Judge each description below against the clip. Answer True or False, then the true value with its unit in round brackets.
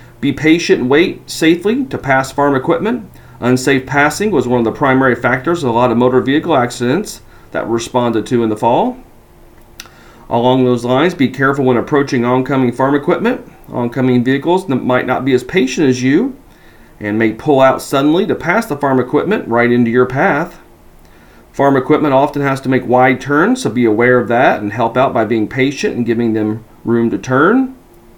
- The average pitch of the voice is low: True (130 Hz)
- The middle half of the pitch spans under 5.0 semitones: True (2.8 semitones)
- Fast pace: False (190 wpm)